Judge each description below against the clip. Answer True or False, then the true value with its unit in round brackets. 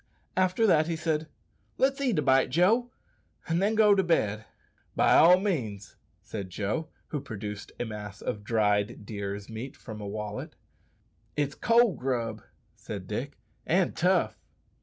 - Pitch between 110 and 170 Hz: True (135 Hz)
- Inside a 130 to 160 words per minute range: True (150 wpm)